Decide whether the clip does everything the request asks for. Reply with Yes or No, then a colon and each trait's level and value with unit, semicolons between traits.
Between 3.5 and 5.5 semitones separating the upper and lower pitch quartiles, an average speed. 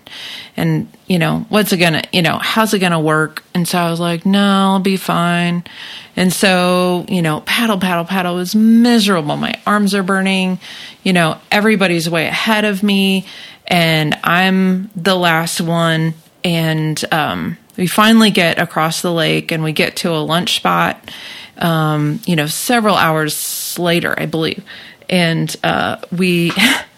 No: average, 2.9 semitones; average, 160 wpm